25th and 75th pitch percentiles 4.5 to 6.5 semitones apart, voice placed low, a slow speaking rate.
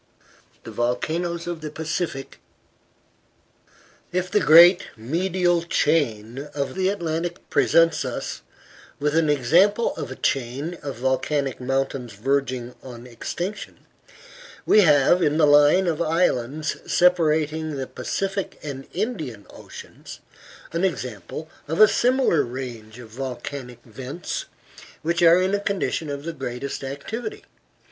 No: average, 4.9 semitones; medium, 150 Hz; slow, 125 wpm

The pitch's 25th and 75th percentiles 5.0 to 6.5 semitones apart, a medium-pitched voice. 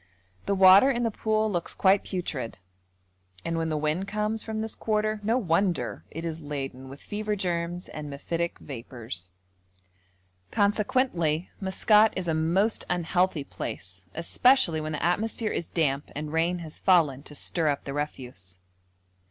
Yes: wide, 5.5 semitones; medium, 170 Hz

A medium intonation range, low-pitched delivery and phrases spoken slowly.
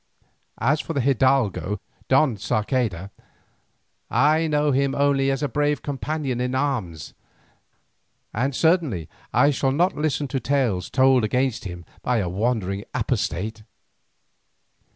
Yes: average, 4.8 semitones; low, 130 Hz; slow, 125 wpm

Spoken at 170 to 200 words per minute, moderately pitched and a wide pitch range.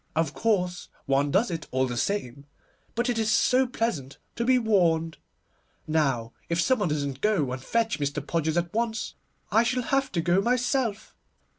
Yes: average, 175 wpm; medium, 180 Hz; wide, 7.8 semitones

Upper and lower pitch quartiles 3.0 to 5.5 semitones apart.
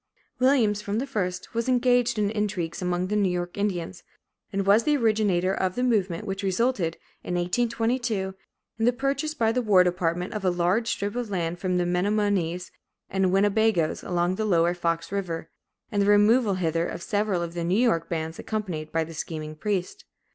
Yes: average, 3.9 semitones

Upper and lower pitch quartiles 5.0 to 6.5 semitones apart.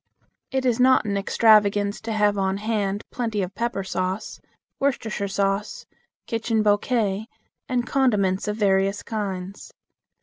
No: narrow, 2.5 semitones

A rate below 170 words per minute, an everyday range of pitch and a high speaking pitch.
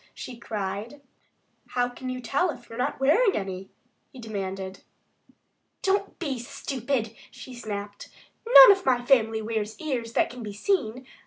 Yes: average, 155 wpm; average, 4.1 semitones; high, 240 Hz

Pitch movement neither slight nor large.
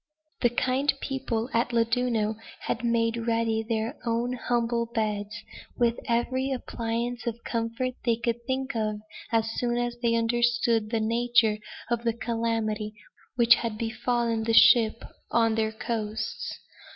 No: narrow, 1.2 semitones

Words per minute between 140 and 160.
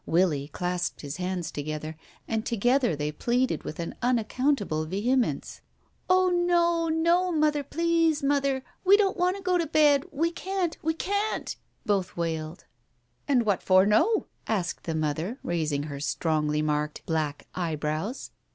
Yes: average, 155 wpm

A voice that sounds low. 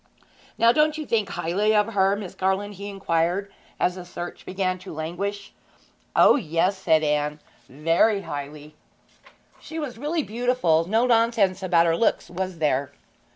No: high, 190 Hz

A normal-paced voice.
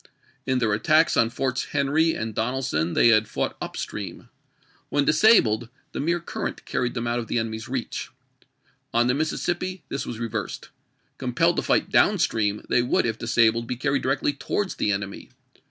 Yes: average, 175 wpm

